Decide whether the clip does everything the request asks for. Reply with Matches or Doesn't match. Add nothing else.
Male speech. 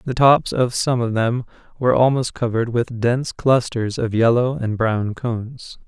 Matches